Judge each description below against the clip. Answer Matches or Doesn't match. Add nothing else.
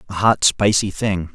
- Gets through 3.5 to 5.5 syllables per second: Matches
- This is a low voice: Matches